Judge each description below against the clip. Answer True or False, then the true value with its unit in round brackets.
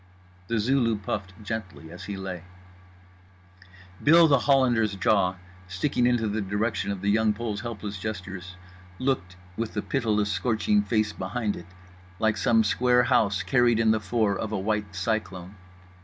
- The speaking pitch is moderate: False (110 Hz)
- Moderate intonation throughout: True (3.3 semitones)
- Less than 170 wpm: True (155 wpm)